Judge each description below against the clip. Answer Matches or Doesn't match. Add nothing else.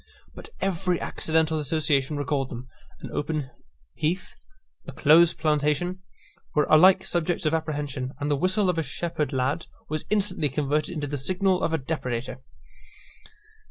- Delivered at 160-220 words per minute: Doesn't match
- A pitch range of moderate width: Matches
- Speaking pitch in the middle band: Matches